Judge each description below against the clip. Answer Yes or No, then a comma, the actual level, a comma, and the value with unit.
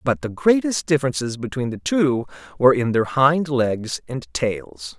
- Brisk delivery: No, average, 170 wpm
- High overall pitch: No, low, 130 Hz